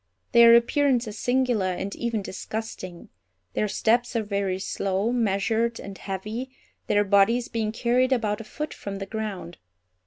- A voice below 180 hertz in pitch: No, high, 220 Hz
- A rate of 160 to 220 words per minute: No, average, 150 wpm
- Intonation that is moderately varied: Yes, average, 3.1 semitones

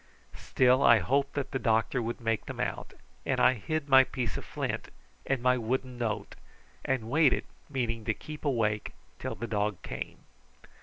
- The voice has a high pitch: No, low, 125 Hz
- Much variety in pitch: No, average, 2.9 semitones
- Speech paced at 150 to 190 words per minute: Yes, average, 170 wpm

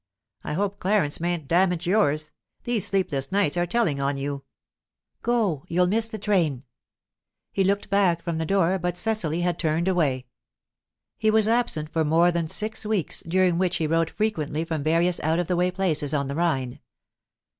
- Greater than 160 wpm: Yes, average, 175 wpm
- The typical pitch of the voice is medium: Yes, medium, 175 Hz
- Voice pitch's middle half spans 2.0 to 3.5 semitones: No, average, 4.1 semitones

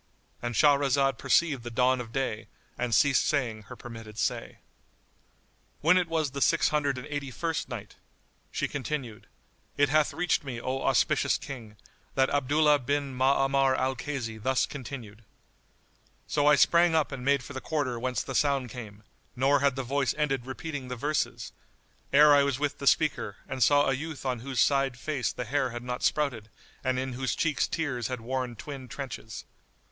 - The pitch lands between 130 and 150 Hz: Yes, low, 135 Hz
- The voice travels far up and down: No, narrow, 2.6 semitones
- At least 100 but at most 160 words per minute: No, average, 175 wpm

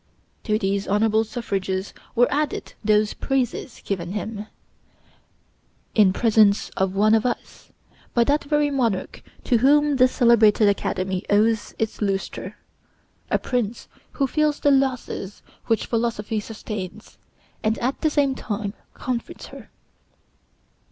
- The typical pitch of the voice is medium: No, high, 220 Hz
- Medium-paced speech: No, slow, 125 wpm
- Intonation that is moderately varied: Yes, average, 3.8 semitones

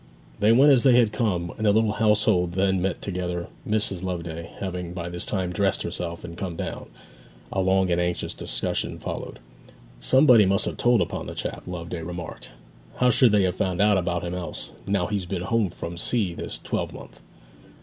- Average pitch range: Yes, average, 3.3 semitones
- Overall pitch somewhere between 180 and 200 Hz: No, very low, 95 Hz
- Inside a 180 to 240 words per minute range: Yes, average, 185 wpm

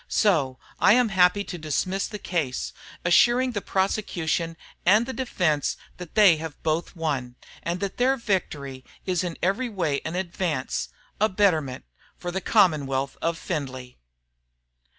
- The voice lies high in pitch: No, medium, 175 Hz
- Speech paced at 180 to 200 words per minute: No, average, 145 wpm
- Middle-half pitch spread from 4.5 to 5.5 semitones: Yes, average, 4.8 semitones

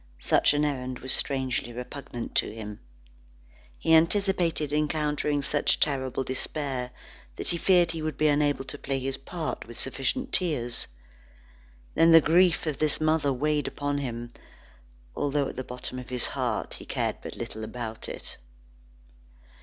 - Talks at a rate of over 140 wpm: Yes, average, 155 wpm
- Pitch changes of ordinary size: Yes, average, 3.5 semitones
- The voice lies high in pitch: No, medium, 145 Hz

